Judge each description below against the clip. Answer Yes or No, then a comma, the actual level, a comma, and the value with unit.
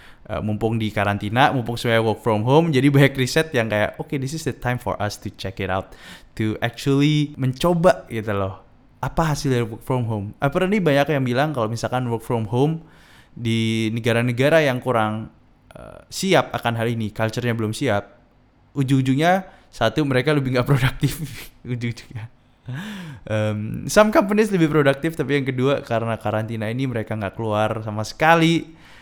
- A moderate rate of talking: No, fast, 170 wpm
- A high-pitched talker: No, low, 120 Hz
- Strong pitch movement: No, average, 4.5 semitones